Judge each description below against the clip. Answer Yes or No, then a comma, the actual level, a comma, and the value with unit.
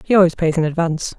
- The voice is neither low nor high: Yes, medium, 170 Hz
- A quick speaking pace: Yes, fast, 255 wpm